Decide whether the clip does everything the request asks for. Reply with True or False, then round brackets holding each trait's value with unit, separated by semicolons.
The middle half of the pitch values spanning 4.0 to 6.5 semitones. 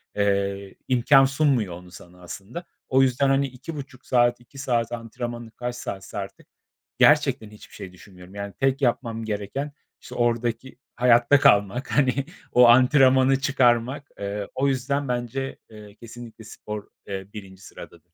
True (4.5 semitones)